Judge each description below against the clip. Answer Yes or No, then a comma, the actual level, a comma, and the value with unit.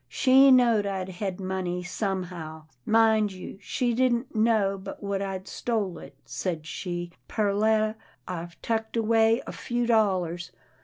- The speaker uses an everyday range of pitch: Yes, average, 3.6 semitones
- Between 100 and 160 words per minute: Yes, average, 150 wpm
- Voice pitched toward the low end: No, high, 200 Hz